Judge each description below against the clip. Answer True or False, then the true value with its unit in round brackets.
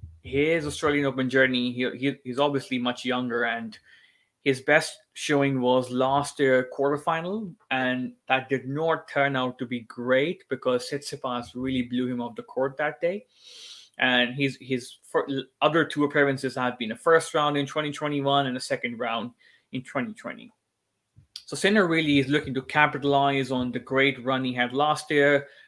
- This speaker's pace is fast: False (170 wpm)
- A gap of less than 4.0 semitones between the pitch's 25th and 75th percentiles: True (2.8 semitones)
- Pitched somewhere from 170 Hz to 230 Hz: False (135 Hz)